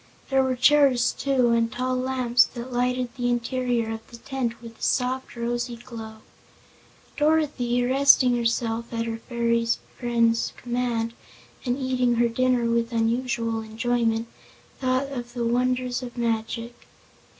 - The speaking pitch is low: No, high, 240 Hz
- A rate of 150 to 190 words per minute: No, average, 140 wpm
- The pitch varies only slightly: Yes, narrow, 1.6 semitones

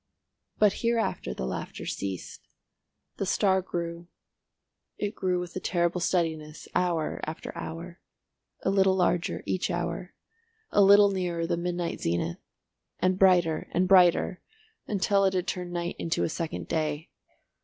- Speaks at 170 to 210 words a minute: No, slow, 135 wpm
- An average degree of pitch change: No, narrow, 2.2 semitones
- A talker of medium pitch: Yes, medium, 175 Hz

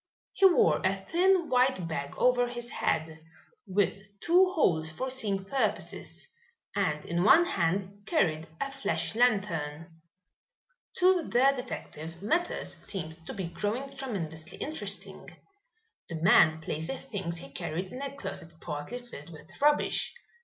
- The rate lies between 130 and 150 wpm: Yes, average, 140 wpm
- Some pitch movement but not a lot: No, wide, 8.4 semitones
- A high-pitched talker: Yes, high, 195 Hz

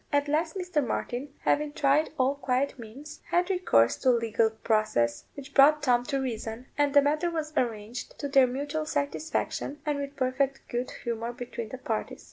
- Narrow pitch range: No, average, 3.5 semitones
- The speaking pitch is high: Yes, very high, 275 Hz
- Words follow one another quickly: No, average, 180 wpm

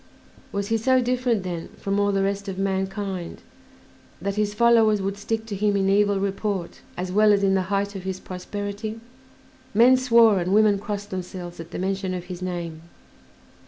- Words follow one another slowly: No, average, 185 wpm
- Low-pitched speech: No, high, 200 Hz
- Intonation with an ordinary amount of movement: No, narrow, 2.0 semitones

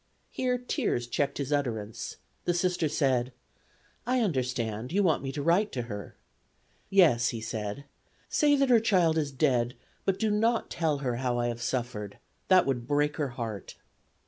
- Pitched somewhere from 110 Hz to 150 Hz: Yes, medium, 140 Hz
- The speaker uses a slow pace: No, average, 170 wpm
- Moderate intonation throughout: No, wide, 7.3 semitones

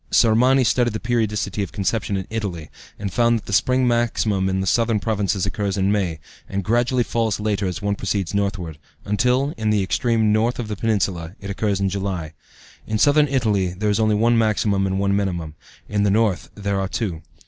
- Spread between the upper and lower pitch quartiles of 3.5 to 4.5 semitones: No, average, 2.7 semitones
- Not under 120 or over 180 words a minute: No, average, 200 wpm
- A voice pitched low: Yes, low, 105 Hz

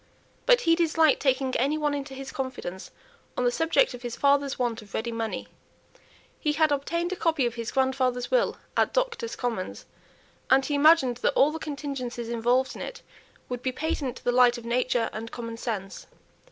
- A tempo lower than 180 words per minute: No, average, 190 wpm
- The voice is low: No, very high, 260 Hz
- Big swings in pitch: No, average, 3.9 semitones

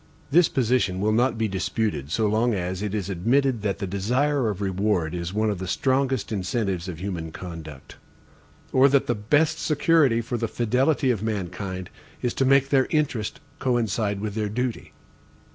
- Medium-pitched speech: No, low, 110 Hz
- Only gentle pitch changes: No, average, 5.1 semitones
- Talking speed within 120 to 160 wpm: No, average, 175 wpm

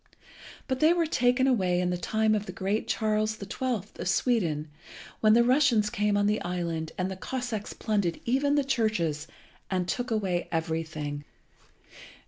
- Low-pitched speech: No, high, 210 Hz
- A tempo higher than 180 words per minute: No, average, 165 wpm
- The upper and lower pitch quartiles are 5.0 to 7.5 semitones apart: Yes, wide, 5.4 semitones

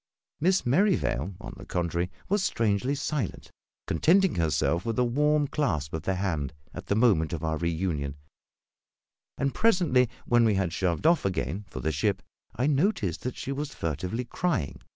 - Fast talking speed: No, average, 165 wpm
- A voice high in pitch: No, low, 105 Hz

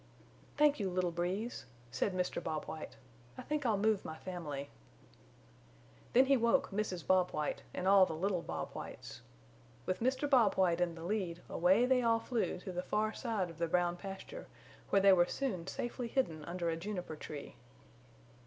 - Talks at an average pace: Yes, average, 180 wpm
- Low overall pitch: No, medium, 185 Hz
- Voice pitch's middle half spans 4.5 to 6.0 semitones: Yes, average, 4.9 semitones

